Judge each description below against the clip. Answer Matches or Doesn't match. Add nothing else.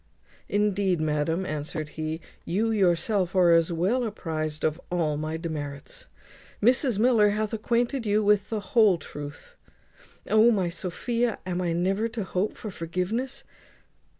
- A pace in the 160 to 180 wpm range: Doesn't match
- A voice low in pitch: Doesn't match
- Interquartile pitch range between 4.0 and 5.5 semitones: Matches